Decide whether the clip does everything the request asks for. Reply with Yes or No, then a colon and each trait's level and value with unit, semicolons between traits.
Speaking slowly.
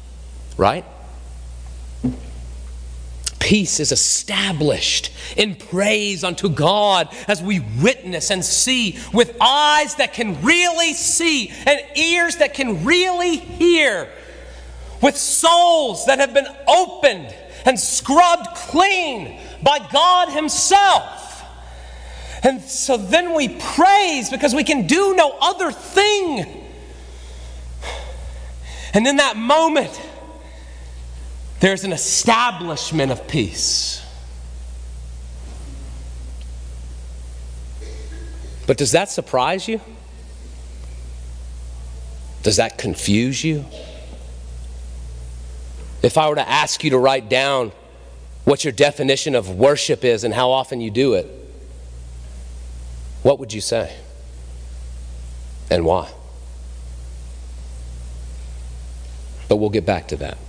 Yes: slow, 100 wpm